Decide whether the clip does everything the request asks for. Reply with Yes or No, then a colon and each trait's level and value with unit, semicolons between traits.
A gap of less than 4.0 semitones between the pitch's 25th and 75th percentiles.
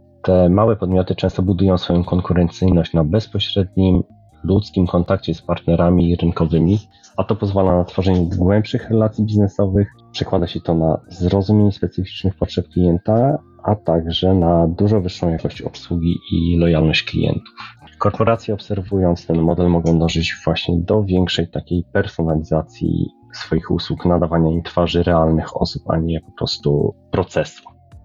Yes: average, 2.9 semitones